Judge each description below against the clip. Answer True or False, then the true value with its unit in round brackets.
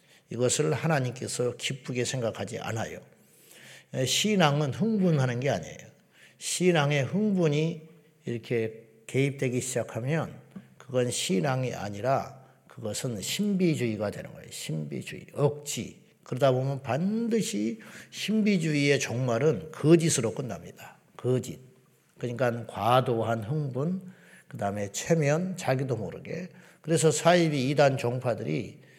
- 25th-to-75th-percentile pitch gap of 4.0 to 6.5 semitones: True (5.2 semitones)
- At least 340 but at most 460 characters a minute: False (275 characters per minute)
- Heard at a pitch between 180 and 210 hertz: False (135 Hz)